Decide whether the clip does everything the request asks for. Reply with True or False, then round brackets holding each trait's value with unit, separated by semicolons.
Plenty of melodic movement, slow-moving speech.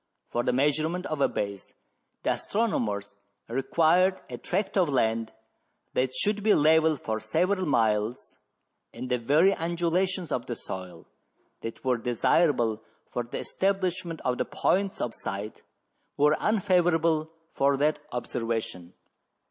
True (7.1 semitones; 130 wpm)